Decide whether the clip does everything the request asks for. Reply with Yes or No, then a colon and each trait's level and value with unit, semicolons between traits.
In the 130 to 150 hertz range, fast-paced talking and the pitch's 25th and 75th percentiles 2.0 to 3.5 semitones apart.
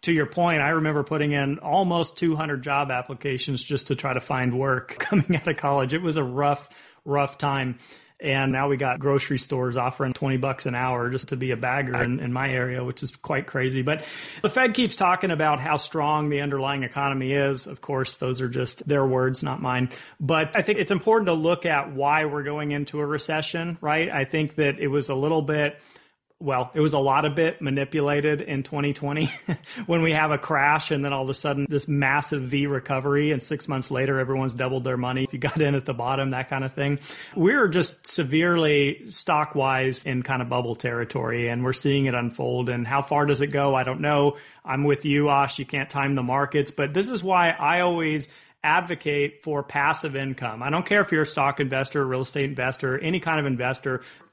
Yes: medium, 140 Hz; fast, 220 wpm; narrow, 2.4 semitones